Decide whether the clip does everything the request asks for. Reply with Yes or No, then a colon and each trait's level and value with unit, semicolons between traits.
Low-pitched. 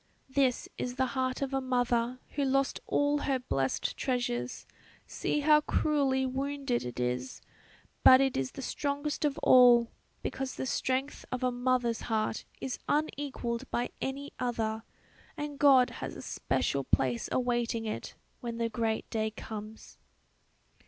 No: very high, 255 Hz